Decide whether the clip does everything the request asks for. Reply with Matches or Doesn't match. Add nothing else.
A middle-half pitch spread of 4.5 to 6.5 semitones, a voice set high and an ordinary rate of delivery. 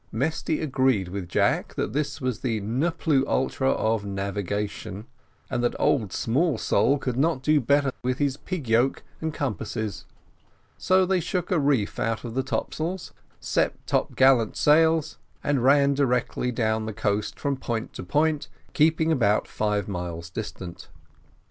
Doesn't match